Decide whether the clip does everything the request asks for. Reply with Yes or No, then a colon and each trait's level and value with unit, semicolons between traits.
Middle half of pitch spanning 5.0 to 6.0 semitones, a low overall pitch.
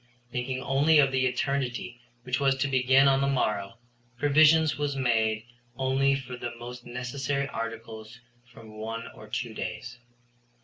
No: average, 2.8 semitones; low, 125 Hz